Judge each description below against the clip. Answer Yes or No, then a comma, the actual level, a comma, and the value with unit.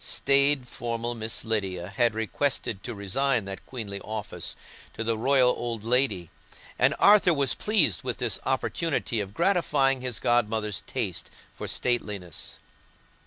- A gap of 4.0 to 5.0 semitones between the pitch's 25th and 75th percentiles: Yes, average, 4.4 semitones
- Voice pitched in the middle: No, low, 120 Hz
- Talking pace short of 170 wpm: Yes, slow, 135 wpm